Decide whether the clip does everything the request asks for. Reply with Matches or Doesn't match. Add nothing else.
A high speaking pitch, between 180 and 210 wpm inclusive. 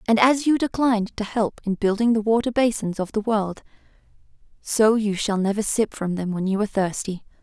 Matches